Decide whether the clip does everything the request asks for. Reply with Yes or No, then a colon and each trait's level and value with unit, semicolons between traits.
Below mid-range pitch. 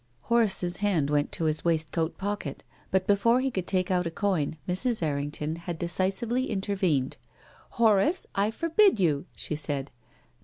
No: medium, 185 Hz